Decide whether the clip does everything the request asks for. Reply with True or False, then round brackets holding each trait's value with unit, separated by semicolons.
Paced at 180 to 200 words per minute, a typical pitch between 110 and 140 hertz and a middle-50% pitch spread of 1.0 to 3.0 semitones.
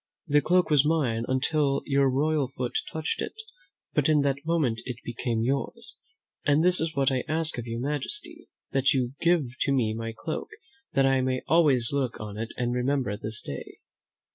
False (185 wpm; 135 Hz; 4.0 semitones)